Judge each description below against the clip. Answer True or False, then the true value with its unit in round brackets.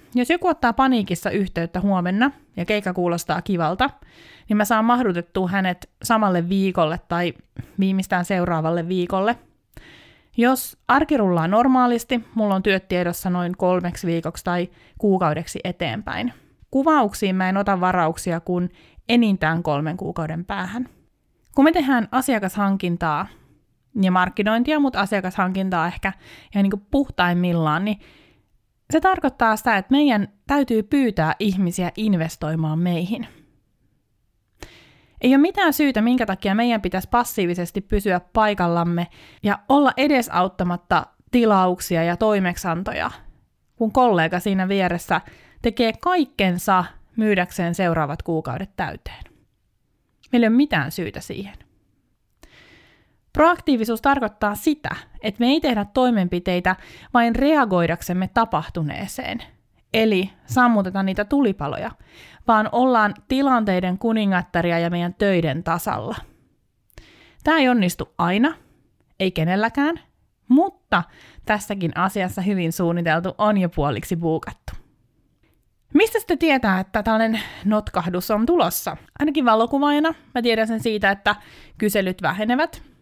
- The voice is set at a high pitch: True (195 Hz)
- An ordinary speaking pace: True (110 wpm)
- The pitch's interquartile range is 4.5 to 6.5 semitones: True (5.2 semitones)